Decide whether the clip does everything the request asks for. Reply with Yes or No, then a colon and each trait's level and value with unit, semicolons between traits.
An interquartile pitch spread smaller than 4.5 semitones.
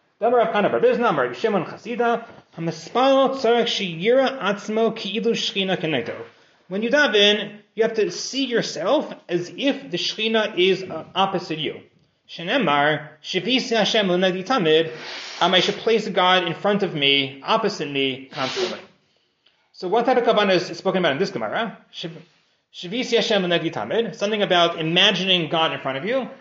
No: average, 5.0 semitones